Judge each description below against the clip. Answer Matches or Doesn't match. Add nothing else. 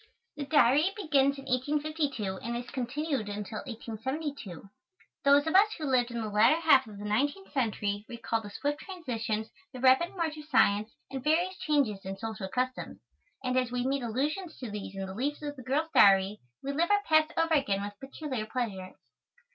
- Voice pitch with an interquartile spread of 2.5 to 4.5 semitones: Doesn't match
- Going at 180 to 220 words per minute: Matches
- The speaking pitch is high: Matches